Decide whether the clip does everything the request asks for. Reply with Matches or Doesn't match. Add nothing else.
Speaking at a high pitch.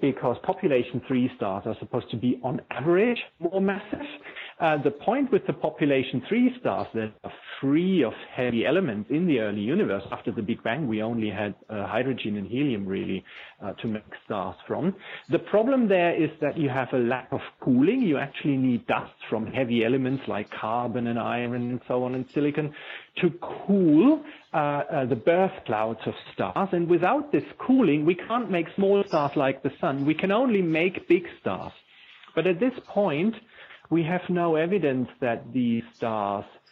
Doesn't match